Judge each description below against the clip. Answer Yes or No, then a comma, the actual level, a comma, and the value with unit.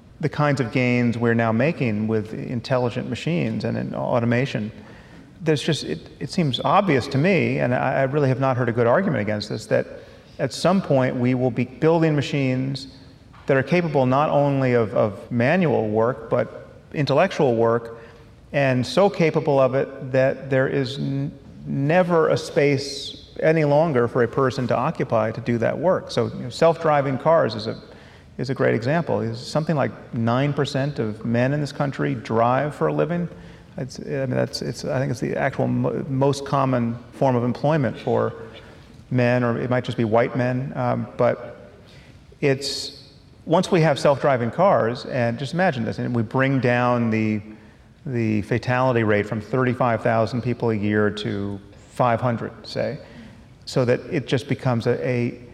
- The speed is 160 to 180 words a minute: Yes, average, 175 wpm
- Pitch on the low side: Yes, low, 125 Hz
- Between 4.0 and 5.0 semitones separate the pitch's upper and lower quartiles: No, average, 3.2 semitones